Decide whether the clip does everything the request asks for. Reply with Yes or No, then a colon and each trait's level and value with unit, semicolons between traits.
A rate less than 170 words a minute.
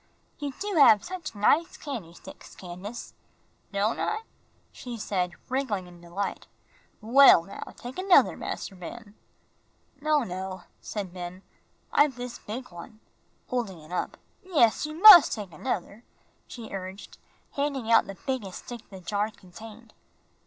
Yes: average, 140 wpm